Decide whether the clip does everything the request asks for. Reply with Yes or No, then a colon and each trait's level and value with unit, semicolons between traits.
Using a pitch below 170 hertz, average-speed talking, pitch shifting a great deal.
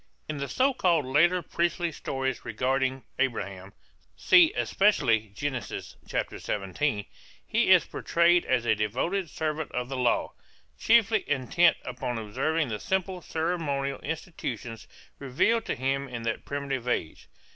No: medium, 140 Hz; slow, 130 wpm; wide, 5.7 semitones